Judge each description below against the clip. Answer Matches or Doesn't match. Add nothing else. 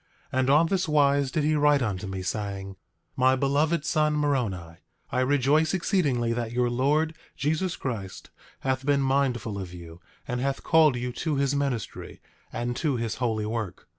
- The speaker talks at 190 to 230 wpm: Doesn't match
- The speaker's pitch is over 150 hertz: Doesn't match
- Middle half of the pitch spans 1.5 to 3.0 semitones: Doesn't match